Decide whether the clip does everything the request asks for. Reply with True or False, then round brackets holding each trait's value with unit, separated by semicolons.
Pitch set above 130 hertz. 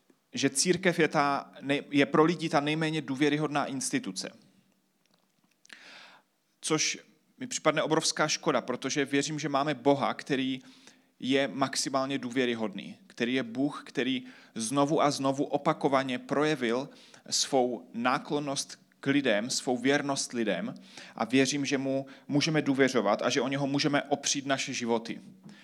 True (140 Hz)